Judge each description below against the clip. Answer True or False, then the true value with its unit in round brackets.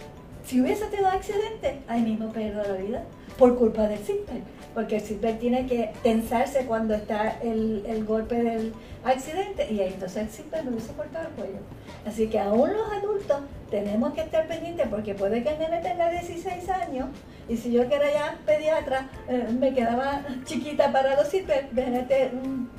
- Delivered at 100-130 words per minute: False (185 wpm)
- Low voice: False (255 Hz)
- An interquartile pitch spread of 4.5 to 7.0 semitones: True (5.5 semitones)